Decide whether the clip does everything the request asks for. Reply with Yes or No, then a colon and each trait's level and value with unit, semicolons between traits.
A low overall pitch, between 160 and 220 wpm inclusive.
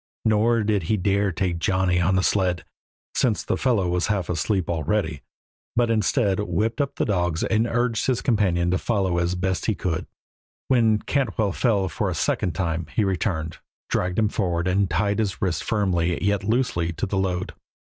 Yes: very low, 95 Hz; average, 180 wpm